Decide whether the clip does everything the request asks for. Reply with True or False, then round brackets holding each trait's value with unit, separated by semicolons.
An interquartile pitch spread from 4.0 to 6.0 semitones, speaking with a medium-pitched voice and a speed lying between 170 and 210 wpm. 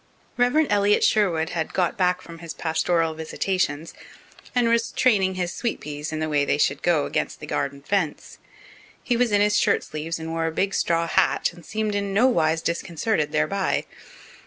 True (4.4 semitones; 170 Hz; 180 wpm)